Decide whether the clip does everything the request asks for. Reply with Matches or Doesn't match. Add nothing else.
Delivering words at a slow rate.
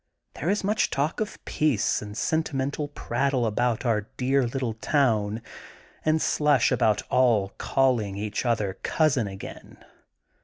Matches